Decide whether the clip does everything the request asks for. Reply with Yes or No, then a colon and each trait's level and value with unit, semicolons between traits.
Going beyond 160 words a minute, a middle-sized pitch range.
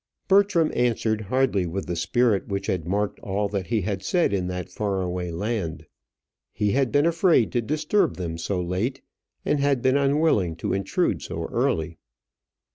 No: average, 170 wpm; wide, 6.6 semitones